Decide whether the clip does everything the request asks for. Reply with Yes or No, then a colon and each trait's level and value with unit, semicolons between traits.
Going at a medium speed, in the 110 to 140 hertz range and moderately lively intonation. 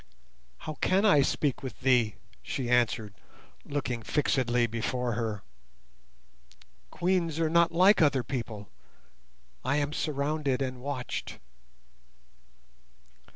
No: slow, 105 wpm; low, 135 Hz; average, 4.1 semitones